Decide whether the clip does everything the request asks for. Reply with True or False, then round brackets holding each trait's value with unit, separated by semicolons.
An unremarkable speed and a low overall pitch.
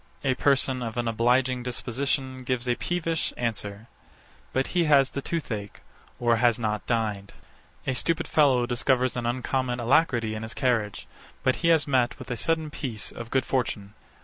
True (170 wpm; 125 Hz)